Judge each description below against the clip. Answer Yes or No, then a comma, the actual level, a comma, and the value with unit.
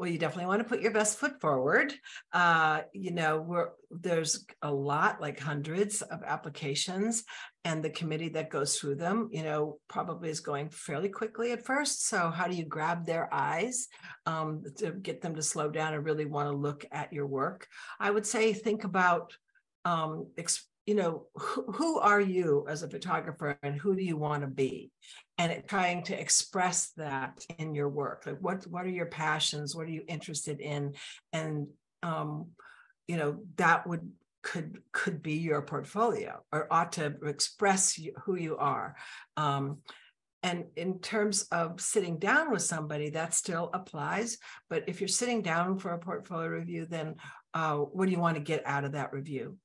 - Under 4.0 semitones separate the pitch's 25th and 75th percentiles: No, average, 4.4 semitones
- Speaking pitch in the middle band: Yes, medium, 165 Hz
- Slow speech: No, average, 185 wpm